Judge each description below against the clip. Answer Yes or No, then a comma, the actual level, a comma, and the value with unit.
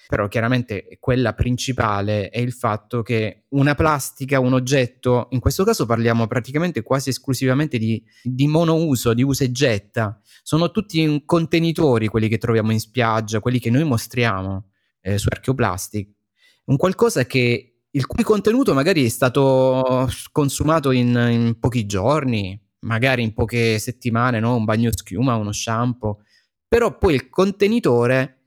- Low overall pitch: Yes, low, 125 Hz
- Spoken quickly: No, average, 145 wpm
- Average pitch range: Yes, average, 3.2 semitones